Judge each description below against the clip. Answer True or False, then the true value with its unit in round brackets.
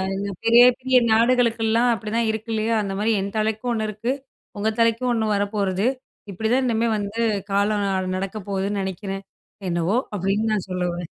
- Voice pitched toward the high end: True (215 Hz)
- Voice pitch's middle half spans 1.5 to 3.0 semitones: True (2.6 semitones)